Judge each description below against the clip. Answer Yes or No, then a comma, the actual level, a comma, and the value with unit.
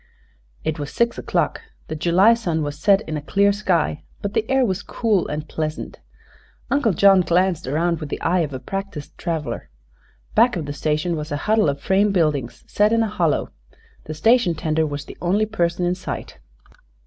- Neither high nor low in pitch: Yes, medium, 175 Hz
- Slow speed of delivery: No, average, 190 wpm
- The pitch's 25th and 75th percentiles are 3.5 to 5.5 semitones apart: Yes, average, 4.8 semitones